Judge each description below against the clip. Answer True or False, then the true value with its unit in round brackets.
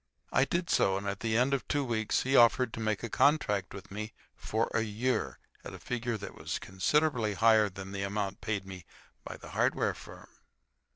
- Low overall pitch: True (110 Hz)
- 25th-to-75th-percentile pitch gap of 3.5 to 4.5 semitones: True (3.8 semitones)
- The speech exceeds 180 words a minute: True (205 wpm)